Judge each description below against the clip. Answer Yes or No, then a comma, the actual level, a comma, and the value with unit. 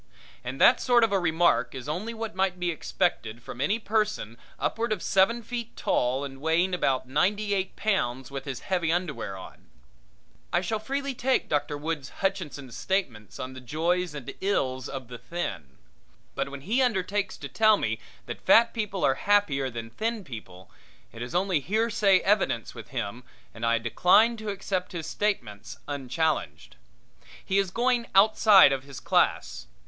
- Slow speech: No, average, 165 wpm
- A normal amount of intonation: No, wide, 7.8 semitones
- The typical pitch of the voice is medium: Yes, medium, 175 Hz